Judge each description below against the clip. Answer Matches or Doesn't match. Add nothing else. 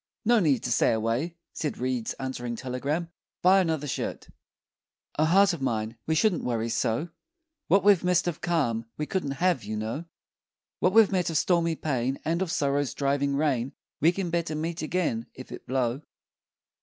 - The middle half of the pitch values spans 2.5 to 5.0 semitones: Doesn't match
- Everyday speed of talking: Matches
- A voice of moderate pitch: Matches